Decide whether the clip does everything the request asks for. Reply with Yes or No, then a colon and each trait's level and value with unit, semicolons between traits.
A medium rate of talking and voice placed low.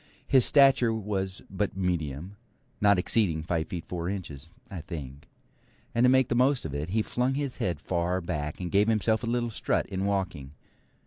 Yes: average, 185 wpm; very low, 95 Hz